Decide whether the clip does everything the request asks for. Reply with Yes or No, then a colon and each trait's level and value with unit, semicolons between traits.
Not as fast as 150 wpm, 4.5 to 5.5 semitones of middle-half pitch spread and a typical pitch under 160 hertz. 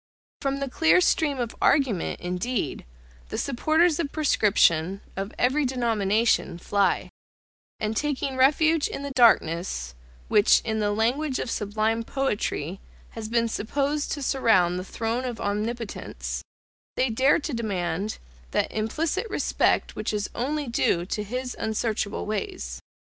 No: slow, 135 wpm; average, 5.0 semitones; high, 230 Hz